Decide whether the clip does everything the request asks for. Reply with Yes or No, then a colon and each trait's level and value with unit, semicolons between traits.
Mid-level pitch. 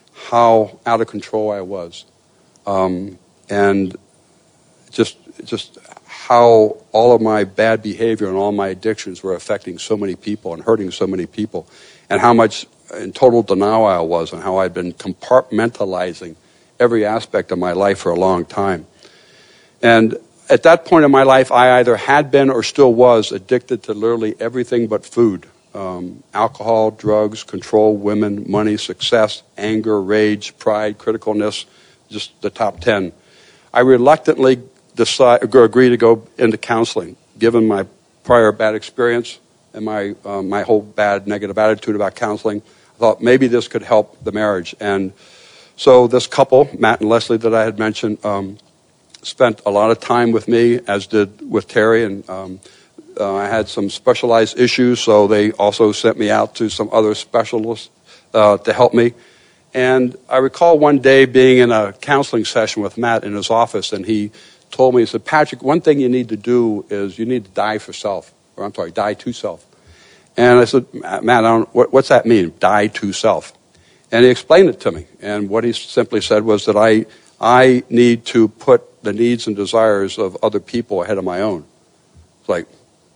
No: low, 110 Hz